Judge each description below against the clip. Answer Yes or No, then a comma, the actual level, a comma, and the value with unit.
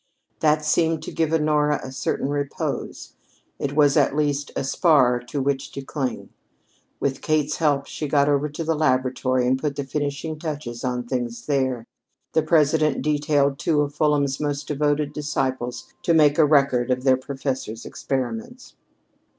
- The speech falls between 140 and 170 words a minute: Yes, average, 160 wpm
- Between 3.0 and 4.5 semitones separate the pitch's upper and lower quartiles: No, narrow, 2.4 semitones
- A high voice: No, medium, 145 Hz